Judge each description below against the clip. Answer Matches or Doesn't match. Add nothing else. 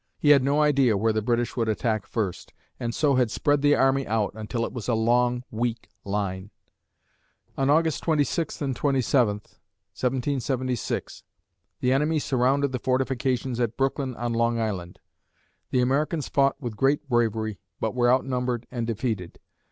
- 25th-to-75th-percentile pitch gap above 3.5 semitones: Doesn't match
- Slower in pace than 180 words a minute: Matches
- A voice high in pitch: Doesn't match